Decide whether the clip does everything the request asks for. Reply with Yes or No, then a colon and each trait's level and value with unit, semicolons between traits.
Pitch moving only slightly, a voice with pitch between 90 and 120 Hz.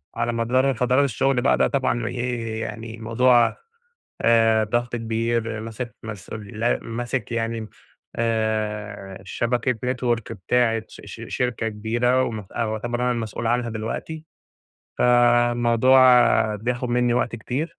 Yes: narrow, 1.6 semitones; low, 115 Hz